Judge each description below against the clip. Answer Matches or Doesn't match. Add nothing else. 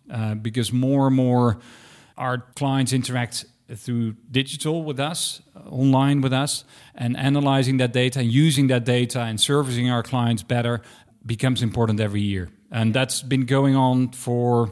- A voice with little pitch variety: Matches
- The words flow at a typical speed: Matches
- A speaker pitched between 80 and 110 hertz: Doesn't match